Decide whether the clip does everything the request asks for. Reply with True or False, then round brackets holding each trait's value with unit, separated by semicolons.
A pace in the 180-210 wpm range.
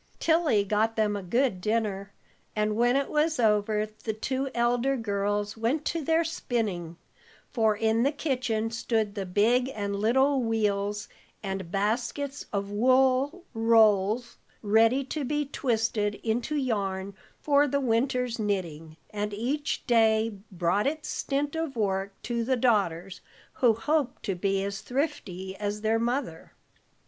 False (140 wpm)